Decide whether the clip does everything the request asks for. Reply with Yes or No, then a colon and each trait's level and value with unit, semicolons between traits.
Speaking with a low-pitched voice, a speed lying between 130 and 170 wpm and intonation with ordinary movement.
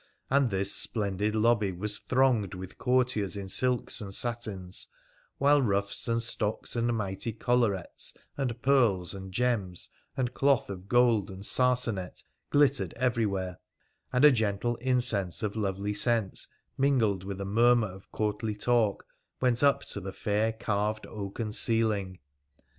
Yes: low, 110 Hz; average, 140 wpm; average, 3.7 semitones